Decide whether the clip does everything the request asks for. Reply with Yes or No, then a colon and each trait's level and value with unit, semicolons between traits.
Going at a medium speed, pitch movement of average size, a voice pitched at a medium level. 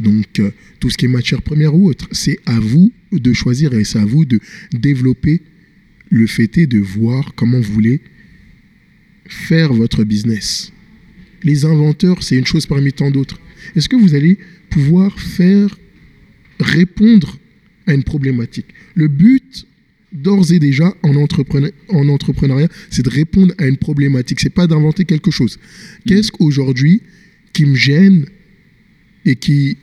No: average, 155 wpm; wide, 5.7 semitones; medium, 155 Hz